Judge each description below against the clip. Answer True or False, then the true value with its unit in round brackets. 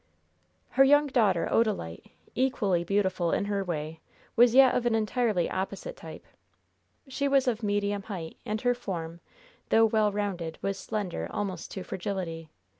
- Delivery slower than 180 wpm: True (150 wpm)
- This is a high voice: True (205 Hz)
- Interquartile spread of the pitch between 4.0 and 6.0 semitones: True (4.7 semitones)